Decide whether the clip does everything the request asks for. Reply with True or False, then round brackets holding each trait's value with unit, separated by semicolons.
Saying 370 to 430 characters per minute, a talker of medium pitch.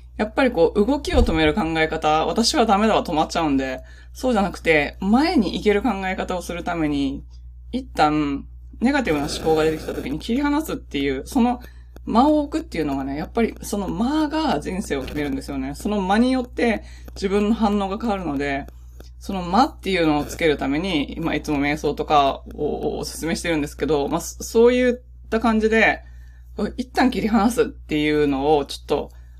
True (380 characters per minute; 165 Hz)